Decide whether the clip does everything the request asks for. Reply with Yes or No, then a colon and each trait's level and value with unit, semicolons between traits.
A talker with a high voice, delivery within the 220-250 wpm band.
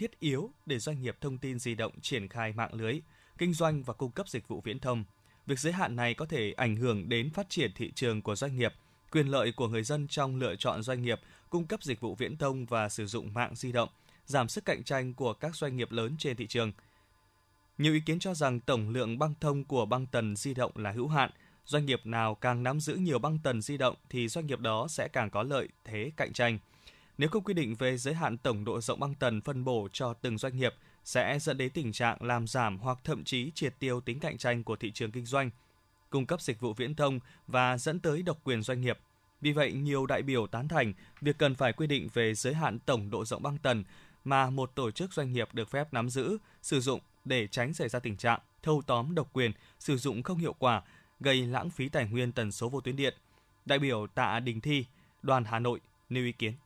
No: low, 125 Hz; average, 245 wpm